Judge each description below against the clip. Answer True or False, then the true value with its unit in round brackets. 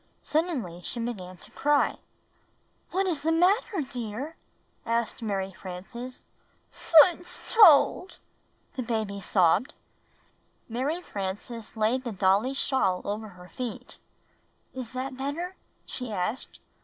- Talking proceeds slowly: True (120 wpm)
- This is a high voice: True (240 Hz)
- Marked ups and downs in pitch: True (6.2 semitones)